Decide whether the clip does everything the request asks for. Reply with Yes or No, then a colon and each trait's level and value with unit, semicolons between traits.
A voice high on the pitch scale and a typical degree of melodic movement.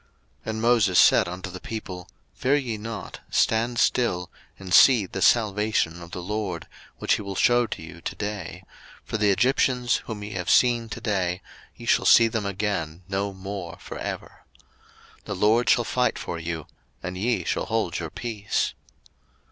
No: low, 105 Hz; average, 4.0 semitones